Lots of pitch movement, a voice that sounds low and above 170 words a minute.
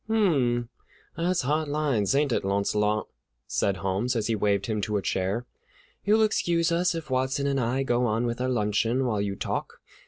Yes: wide, 5.9 semitones; low, 120 Hz; average, 185 wpm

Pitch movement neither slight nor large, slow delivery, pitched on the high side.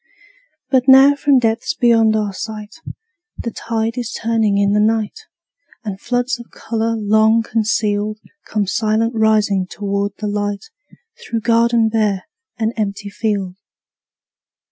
No: narrow, 1.9 semitones; slow, 130 wpm; high, 220 Hz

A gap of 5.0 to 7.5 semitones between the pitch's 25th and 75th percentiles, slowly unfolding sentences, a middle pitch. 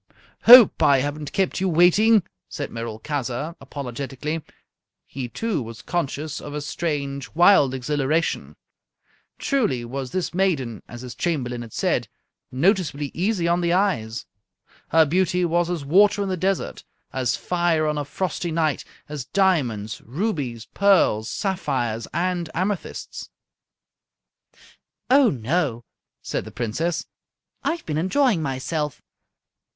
Yes: wide, 5.5 semitones; slow, 125 wpm; medium, 155 Hz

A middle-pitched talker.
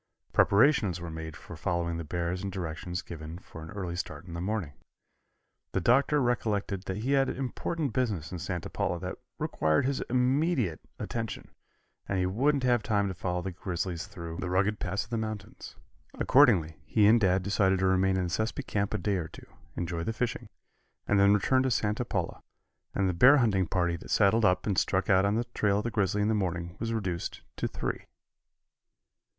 No: very low, 95 Hz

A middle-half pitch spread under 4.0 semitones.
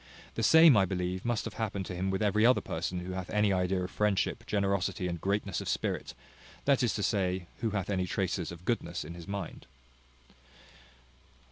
Yes: narrow, 2.6 semitones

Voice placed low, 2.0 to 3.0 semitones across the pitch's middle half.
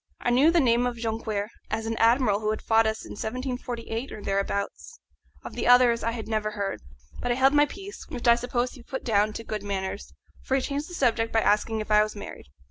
No: high, 230 Hz; average, 2.7 semitones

